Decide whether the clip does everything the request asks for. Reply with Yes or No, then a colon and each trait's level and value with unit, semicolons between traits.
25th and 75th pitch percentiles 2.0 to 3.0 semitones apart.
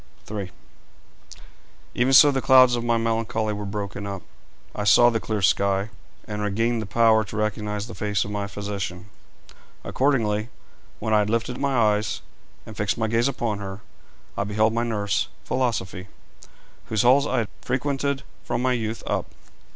Yes: average, 2.7 semitones